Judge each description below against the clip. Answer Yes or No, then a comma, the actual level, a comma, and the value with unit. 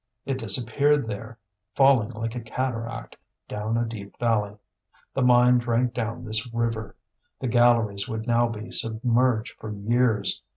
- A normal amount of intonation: No, narrow, 1.9 semitones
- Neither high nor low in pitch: No, low, 115 Hz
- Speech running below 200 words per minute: Yes, average, 140 wpm